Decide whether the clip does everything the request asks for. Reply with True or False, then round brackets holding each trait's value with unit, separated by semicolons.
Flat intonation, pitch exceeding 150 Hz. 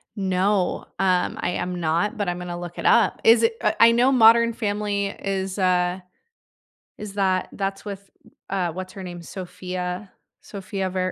True (2.3 semitones; 190 Hz)